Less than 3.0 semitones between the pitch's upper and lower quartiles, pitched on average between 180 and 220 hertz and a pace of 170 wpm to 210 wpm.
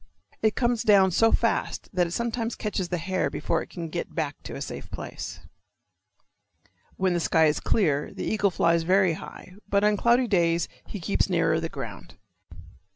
No: average, 4.3 semitones; medium, 185 Hz; average, 180 wpm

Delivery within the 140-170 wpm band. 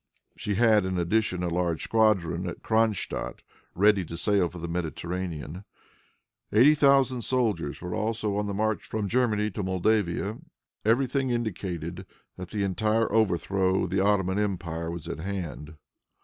Yes: average, 150 wpm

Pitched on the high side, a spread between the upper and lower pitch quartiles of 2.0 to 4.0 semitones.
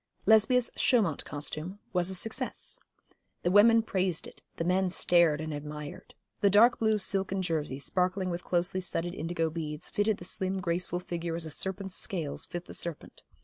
No: medium, 180 Hz; average, 2.8 semitones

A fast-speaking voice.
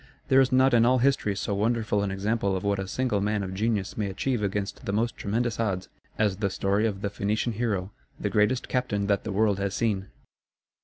Yes: fast, 215 wpm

